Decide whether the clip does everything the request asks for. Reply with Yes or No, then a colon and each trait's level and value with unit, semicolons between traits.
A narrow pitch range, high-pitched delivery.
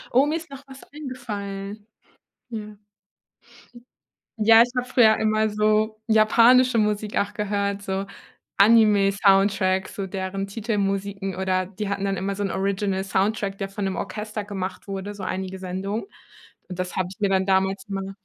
Yes: narrow, 1.8 semitones; high, 200 Hz